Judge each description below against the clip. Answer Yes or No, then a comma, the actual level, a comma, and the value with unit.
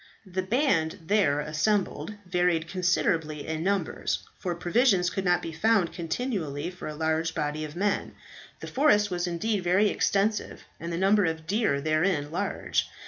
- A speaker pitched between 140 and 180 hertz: Yes, medium, 175 Hz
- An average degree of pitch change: Yes, average, 4.0 semitones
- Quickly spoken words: No, average, 155 wpm